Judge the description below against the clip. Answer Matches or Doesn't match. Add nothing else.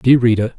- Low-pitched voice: Matches